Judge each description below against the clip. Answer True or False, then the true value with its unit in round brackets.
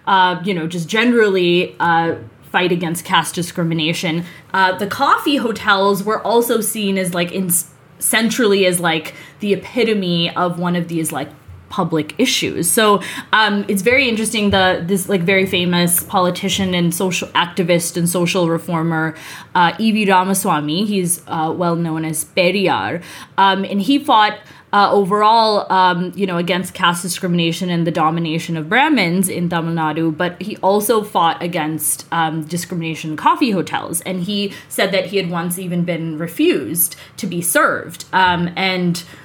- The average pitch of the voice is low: False (180 Hz)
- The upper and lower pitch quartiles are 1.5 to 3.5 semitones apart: True (3.0 semitones)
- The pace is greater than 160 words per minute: False (155 wpm)